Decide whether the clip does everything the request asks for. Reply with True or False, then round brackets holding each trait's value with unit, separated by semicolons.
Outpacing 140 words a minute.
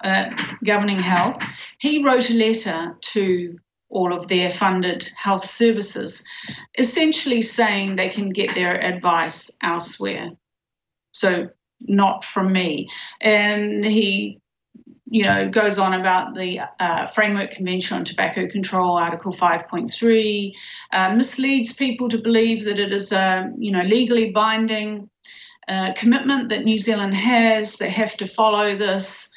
False (135 wpm)